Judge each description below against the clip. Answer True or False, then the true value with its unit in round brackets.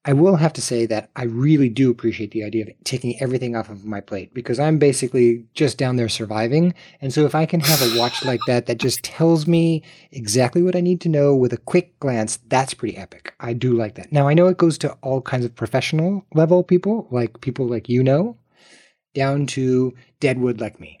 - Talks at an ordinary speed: False (225 wpm)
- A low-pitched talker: True (130 Hz)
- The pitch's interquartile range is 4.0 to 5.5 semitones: True (4.8 semitones)